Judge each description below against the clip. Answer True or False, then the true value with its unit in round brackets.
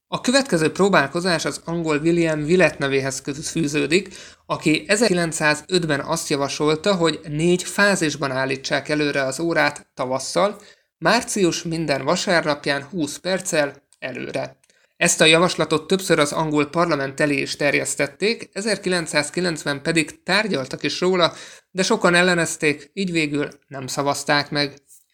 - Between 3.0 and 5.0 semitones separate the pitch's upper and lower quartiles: True (3.4 semitones)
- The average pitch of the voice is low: False (160 Hz)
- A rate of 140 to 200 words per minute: False (120 wpm)